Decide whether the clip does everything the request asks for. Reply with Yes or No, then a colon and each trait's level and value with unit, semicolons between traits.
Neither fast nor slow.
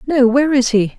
No: fast, 245 wpm